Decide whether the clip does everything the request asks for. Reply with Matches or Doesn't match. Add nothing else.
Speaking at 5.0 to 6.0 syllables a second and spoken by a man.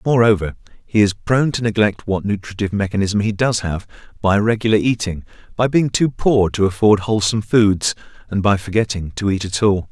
Matches